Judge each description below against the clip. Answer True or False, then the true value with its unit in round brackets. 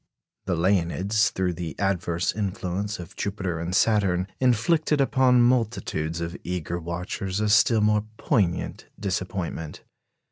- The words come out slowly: True (120 wpm)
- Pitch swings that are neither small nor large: True (3.6 semitones)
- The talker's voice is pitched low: True (95 Hz)